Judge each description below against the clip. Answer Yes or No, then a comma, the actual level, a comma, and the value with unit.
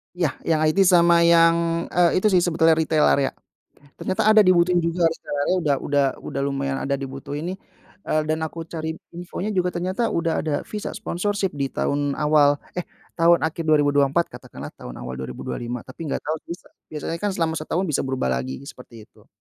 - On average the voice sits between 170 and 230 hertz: No, medium, 160 Hz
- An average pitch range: Yes, average, 3.4 semitones